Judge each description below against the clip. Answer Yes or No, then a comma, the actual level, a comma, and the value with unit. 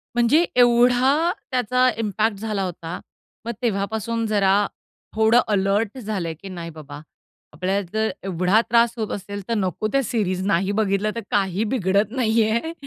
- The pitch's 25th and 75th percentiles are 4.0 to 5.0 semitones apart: No, average, 3.2 semitones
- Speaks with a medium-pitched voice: No, high, 215 Hz